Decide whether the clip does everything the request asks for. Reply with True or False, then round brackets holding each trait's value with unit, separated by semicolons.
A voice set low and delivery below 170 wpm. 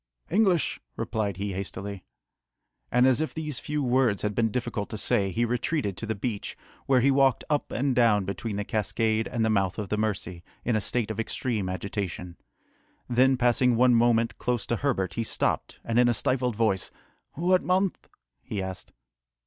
False (115 Hz; 180 wpm)